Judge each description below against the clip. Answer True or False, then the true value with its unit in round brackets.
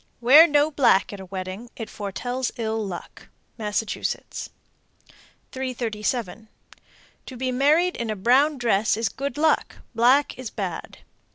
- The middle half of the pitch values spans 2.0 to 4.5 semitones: True (4.0 semitones)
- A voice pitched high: True (235 Hz)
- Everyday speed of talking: False (130 wpm)